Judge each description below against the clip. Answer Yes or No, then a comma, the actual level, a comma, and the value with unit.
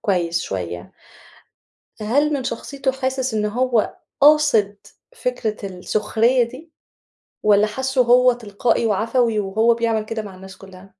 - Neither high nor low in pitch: No, high, 225 Hz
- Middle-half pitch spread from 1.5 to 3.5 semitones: No, average, 4.0 semitones